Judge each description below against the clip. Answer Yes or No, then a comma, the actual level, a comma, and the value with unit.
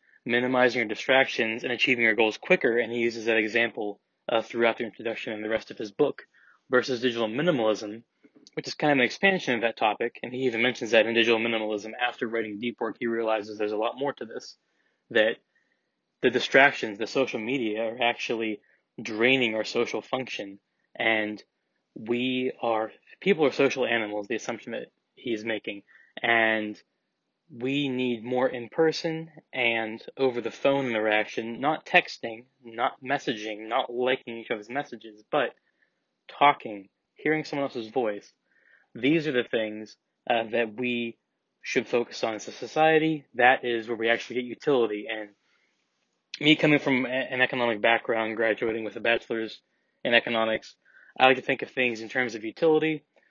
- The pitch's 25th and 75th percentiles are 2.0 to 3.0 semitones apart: Yes, average, 2.7 semitones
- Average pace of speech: Yes, average, 165 wpm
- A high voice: No, low, 120 Hz